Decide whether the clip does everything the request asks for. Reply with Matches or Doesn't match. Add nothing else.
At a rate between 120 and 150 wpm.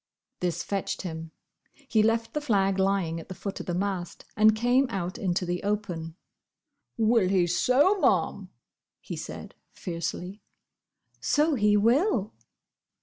Matches